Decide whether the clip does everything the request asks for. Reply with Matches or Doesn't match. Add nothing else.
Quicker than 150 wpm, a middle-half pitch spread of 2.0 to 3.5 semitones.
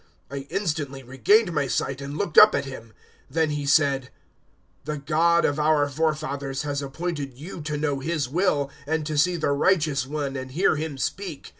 Matches